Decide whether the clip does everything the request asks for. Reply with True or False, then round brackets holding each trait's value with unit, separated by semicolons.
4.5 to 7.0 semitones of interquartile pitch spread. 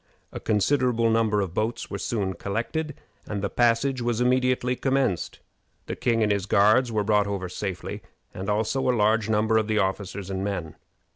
False (3.3 semitones)